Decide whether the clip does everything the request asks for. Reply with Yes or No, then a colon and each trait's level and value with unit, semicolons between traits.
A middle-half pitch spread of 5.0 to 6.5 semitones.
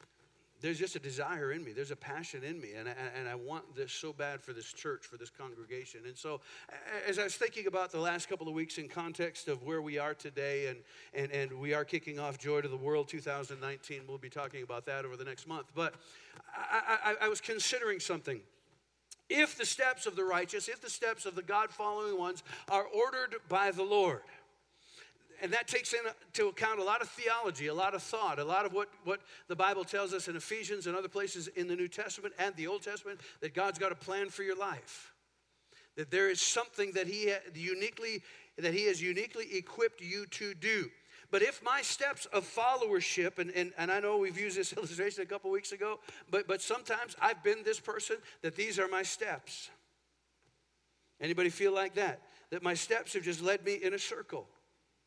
Yes: average, 5.3 semitones